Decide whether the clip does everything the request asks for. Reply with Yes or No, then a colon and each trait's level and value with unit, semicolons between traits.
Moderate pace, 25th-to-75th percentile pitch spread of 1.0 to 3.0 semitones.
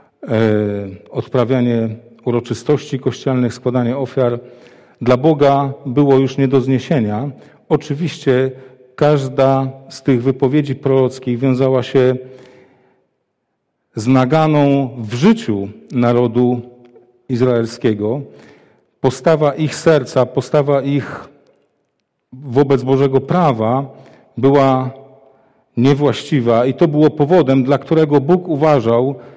No: slow, 90 wpm; narrow, 2.4 semitones